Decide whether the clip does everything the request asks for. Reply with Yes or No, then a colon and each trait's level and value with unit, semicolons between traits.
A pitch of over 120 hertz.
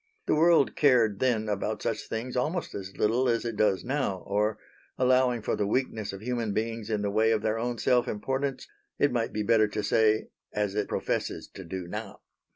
No: low, 110 Hz